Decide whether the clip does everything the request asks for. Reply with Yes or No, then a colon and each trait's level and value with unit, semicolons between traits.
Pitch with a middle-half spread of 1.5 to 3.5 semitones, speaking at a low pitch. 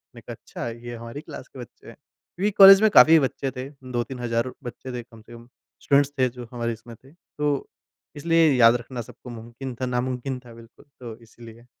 Yes: narrow, 2.6 semitones; low, 125 Hz